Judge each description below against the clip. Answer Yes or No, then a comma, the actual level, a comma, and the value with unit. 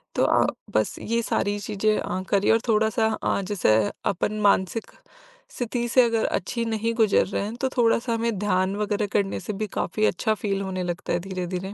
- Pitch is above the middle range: Yes, high, 210 Hz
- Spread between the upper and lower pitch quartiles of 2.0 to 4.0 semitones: Yes, average, 2.8 semitones